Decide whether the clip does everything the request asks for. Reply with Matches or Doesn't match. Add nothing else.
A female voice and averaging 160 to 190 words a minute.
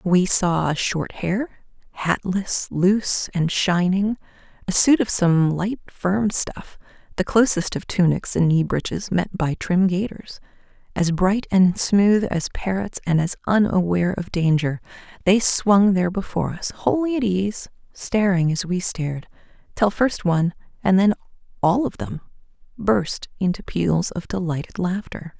Doesn't match